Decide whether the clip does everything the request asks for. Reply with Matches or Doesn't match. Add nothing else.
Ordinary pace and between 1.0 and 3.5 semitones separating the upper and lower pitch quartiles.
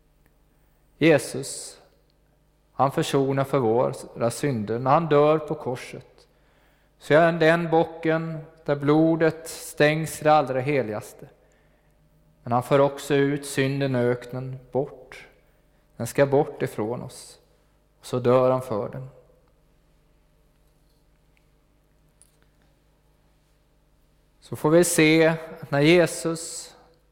Doesn't match